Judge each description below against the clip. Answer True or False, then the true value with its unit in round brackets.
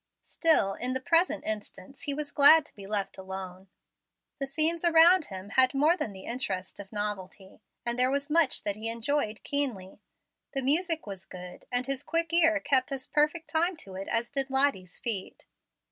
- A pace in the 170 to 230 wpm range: True (185 wpm)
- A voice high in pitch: True (260 Hz)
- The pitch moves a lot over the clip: True (7.1 semitones)